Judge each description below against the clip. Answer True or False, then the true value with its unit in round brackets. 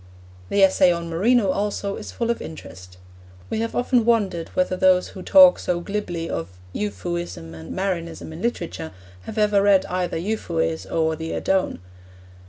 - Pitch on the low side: False (185 Hz)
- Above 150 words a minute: True (160 wpm)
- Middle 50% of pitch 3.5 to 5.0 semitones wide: True (4.0 semitones)